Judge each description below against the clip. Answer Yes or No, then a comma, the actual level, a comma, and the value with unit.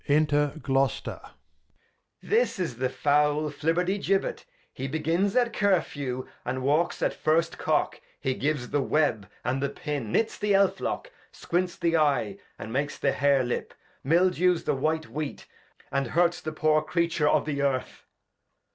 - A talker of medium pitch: Yes, medium, 150 Hz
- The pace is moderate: Yes, average, 155 wpm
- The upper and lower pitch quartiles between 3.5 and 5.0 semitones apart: Yes, average, 3.9 semitones